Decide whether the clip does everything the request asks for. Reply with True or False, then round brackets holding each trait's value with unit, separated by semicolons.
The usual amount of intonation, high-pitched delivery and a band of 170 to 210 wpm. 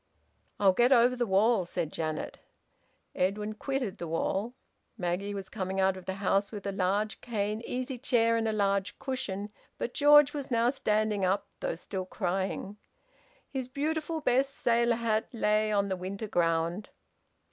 False (4.1 semitones; 210 Hz; 160 wpm)